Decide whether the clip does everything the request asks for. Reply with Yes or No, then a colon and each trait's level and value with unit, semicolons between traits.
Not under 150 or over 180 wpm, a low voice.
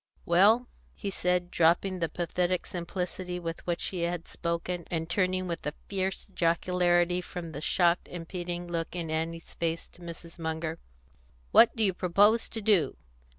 No: average, 160 wpm; medium, 175 Hz